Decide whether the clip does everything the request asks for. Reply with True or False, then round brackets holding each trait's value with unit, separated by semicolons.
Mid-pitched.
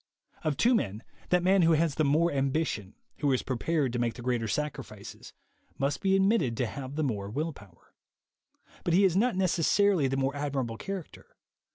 True (145 Hz)